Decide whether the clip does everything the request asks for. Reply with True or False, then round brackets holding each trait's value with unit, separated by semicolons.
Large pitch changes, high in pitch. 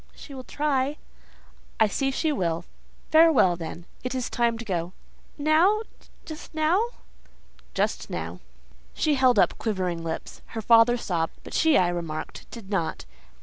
True (8.9 semitones; 235 Hz)